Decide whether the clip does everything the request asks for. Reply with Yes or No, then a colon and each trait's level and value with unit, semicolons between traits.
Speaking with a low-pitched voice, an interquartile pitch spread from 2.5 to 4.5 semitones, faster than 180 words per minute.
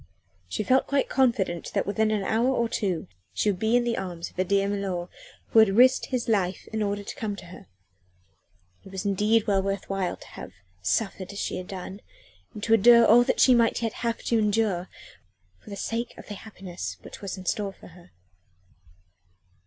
No: high, 205 Hz; average, 3.0 semitones; average, 200 wpm